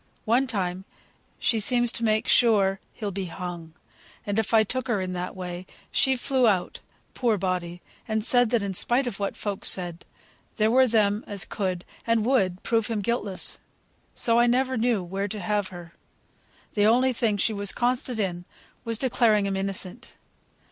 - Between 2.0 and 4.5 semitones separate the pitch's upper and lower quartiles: Yes, average, 3.9 semitones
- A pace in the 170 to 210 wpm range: Yes, average, 175 wpm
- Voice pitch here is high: Yes, high, 210 Hz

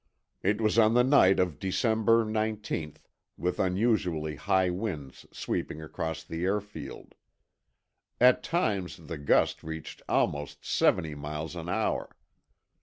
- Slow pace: Yes, slow, 120 wpm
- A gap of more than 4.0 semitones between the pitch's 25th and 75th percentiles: Yes, wide, 5.4 semitones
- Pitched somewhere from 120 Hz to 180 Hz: No, very low, 90 Hz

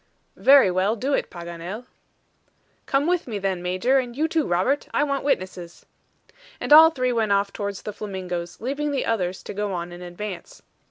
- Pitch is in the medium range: No, high, 205 Hz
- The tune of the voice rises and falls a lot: Yes, wide, 6.9 semitones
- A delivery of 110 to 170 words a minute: No, average, 180 wpm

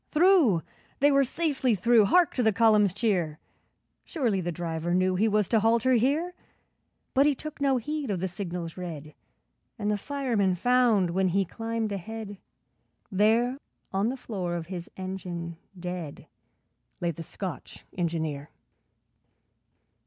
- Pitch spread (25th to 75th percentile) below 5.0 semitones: No, wide, 5.6 semitones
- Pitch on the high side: Yes, high, 205 Hz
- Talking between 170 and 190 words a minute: No, average, 145 wpm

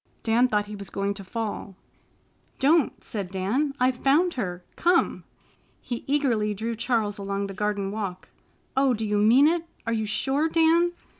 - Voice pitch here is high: Yes, high, 225 Hz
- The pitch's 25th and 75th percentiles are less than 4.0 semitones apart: No, average, 5.2 semitones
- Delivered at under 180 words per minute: Yes, average, 165 wpm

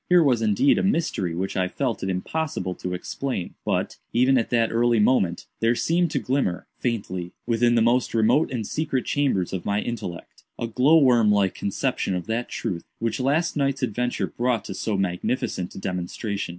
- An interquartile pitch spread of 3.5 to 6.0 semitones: Yes, average, 5.3 semitones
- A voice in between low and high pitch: No, low, 115 Hz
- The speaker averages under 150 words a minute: No, average, 185 wpm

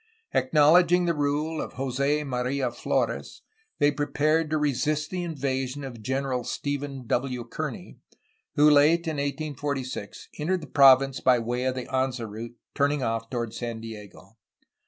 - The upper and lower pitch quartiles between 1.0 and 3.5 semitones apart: Yes, average, 3.1 semitones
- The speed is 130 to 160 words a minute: Yes, average, 150 wpm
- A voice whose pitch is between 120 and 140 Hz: Yes, low, 135 Hz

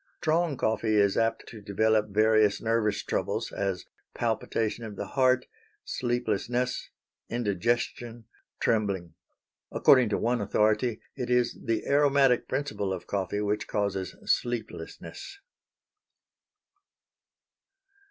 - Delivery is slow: Yes, slow, 105 wpm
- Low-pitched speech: Yes, low, 110 Hz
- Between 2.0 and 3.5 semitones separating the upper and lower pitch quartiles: Yes, average, 3.1 semitones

